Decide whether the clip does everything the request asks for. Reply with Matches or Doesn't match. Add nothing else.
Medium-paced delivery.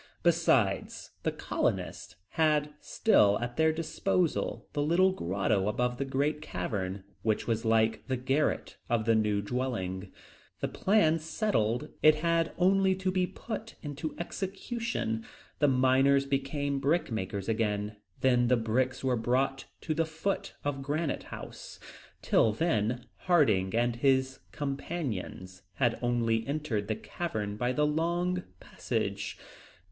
Doesn't match